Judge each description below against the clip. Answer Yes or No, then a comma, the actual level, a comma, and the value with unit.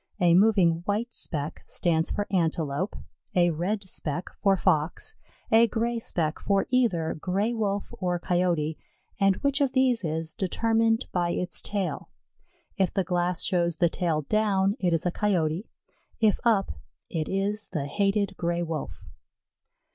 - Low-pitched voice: No, medium, 185 Hz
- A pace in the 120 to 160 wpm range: Yes, average, 145 wpm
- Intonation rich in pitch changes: No, average, 3.7 semitones